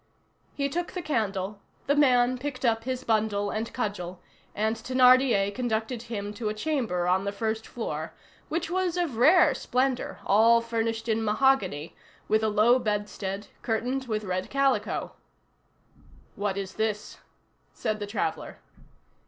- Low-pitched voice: No, high, 225 Hz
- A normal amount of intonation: Yes, average, 3.7 semitones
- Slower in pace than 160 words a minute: Yes, average, 145 wpm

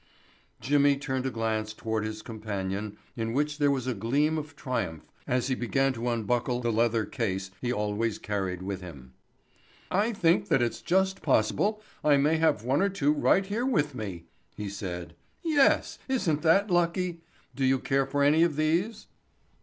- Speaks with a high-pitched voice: No, low, 130 Hz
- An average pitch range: No, wide, 6.3 semitones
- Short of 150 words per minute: No, average, 175 wpm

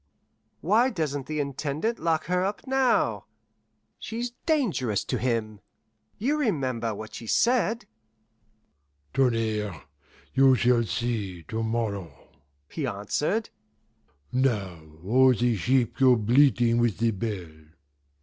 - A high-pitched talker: No, low, 125 Hz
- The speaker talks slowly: Yes, slow, 110 wpm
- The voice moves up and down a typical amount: No, wide, 6.6 semitones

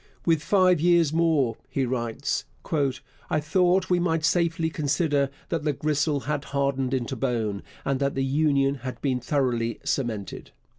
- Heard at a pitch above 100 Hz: Yes, medium, 140 Hz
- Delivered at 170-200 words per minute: No, average, 150 wpm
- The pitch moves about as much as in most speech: Yes, average, 3.7 semitones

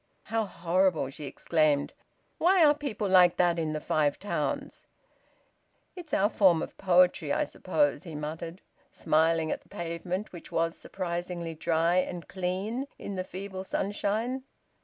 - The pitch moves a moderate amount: Yes, average, 3.4 semitones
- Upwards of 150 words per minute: No, average, 145 wpm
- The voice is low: No, medium, 180 Hz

